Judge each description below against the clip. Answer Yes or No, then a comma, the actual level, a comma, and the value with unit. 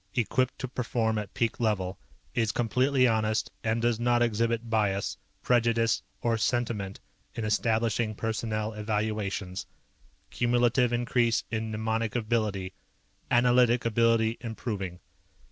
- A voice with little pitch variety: Yes, narrow, 1.8 semitones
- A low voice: Yes, low, 115 Hz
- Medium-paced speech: No, slow, 110 wpm